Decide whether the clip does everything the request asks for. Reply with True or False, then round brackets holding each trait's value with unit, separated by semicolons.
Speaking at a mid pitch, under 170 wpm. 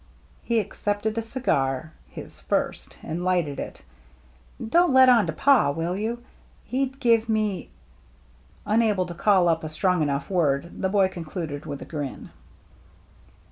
True (180 Hz; 160 wpm)